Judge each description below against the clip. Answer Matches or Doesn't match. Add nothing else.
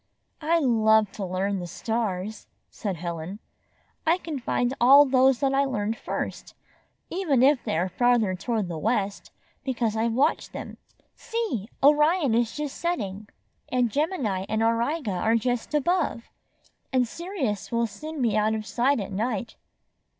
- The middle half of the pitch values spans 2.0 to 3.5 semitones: Doesn't match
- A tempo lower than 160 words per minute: Matches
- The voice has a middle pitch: Doesn't match